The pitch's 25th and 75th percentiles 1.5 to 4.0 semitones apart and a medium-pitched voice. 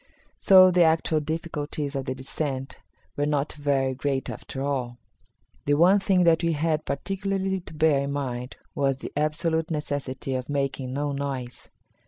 Yes: average, 3.0 semitones; medium, 145 Hz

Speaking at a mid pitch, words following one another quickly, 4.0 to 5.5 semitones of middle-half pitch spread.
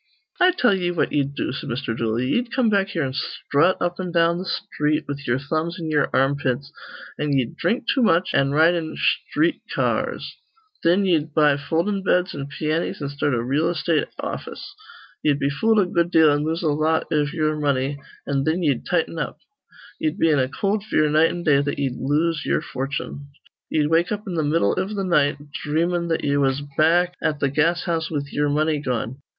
No: medium, 155 Hz; fast, 210 wpm; average, 3.5 semitones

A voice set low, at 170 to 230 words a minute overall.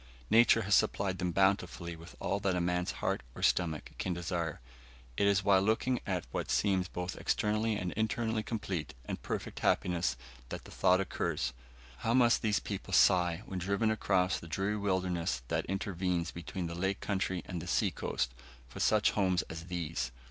Yes: very low, 95 Hz; average, 175 wpm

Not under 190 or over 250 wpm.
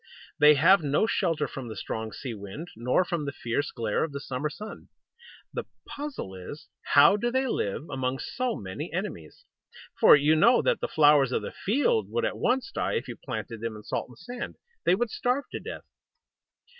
Yes: average, 195 wpm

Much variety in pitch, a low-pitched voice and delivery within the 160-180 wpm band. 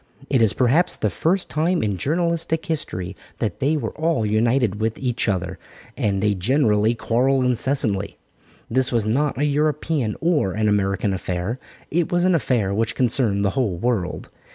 Yes: wide, 6.3 semitones; low, 120 Hz; average, 165 wpm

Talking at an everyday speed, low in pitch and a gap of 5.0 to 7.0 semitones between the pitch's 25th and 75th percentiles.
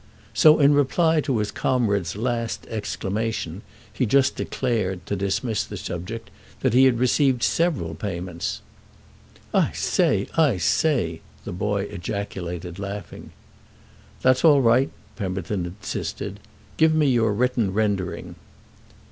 No: slow, 120 wpm; low, 110 Hz; average, 5.3 semitones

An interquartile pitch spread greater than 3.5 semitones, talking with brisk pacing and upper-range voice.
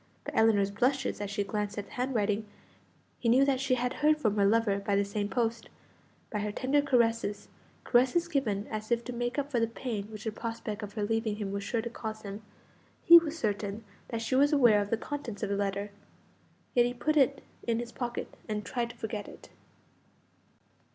No: average, 3.2 semitones; fast, 210 wpm; high, 225 Hz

